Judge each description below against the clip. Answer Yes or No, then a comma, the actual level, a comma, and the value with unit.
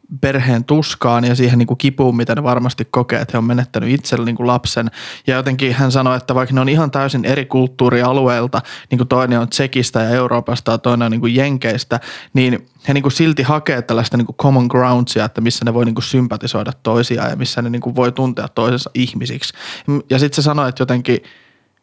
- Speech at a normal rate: No, fast, 210 wpm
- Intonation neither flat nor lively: No, narrow, 2.1 semitones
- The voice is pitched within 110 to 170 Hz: Yes, low, 125 Hz